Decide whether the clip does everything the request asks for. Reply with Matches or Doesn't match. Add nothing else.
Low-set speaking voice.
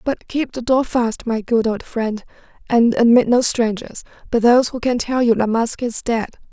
Doesn't match